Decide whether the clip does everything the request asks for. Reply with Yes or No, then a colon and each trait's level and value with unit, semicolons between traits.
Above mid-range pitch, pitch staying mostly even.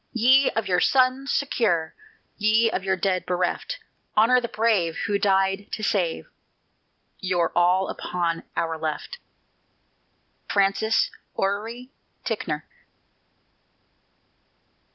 No: high, 200 Hz; average, 4.2 semitones